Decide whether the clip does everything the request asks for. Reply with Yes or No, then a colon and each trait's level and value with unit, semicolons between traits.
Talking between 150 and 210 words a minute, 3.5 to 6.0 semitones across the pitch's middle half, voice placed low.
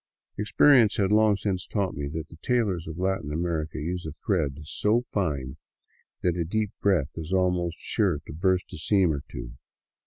Yes: average, 185 wpm; average, 4.3 semitones; very low, 90 Hz